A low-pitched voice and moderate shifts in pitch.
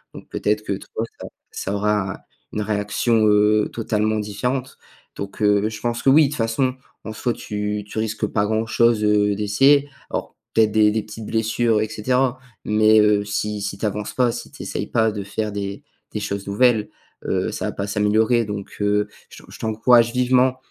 No: low, 110 Hz; narrow, 2.0 semitones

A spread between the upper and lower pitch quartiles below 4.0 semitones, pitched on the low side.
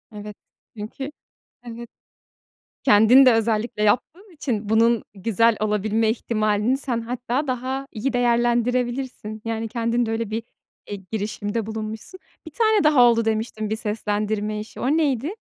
No: average, 2.7 semitones; high, 230 Hz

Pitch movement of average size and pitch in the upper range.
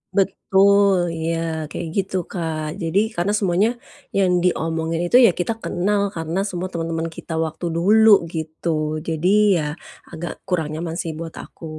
No: average, 3.0 semitones; medium, 175 Hz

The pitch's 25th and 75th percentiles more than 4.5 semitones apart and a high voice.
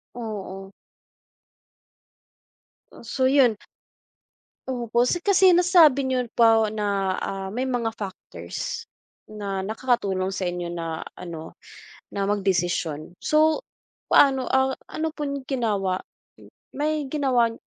Yes: wide, 5.6 semitones; high, 230 Hz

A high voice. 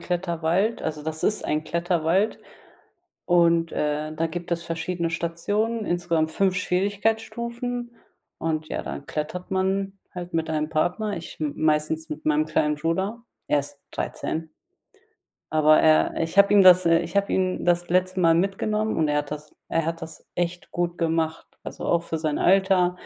No: medium, 170 Hz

